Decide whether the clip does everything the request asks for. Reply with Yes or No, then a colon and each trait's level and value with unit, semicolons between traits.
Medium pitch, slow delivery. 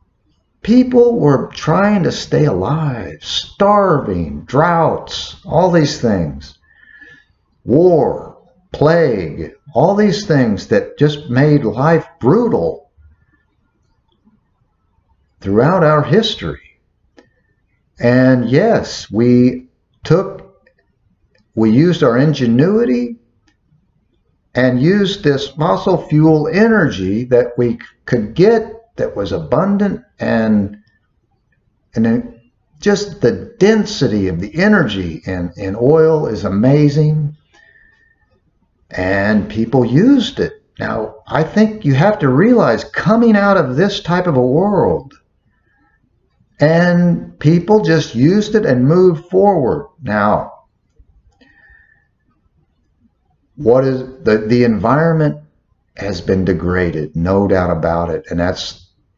Yes: medium, 145 Hz; slow, 100 wpm